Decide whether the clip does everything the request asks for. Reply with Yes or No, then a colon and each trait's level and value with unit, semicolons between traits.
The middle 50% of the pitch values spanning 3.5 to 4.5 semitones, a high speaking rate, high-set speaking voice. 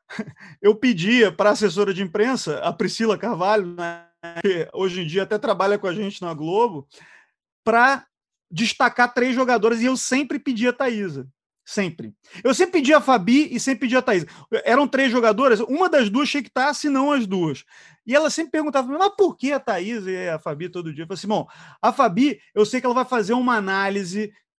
No: average, 5.3 semitones; fast, 205 wpm; high, 230 Hz